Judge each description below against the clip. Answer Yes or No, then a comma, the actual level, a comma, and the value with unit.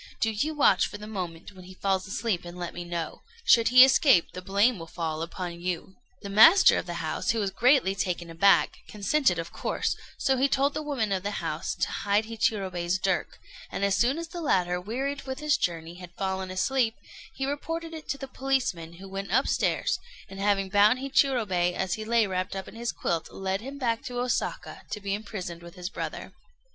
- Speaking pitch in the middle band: No, high, 200 Hz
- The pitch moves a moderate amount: No, wide, 5.7 semitones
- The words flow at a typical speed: No, fast, 210 wpm